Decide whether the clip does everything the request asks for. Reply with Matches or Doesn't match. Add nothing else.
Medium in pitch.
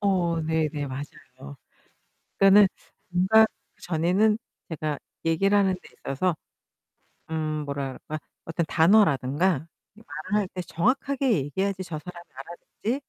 Matches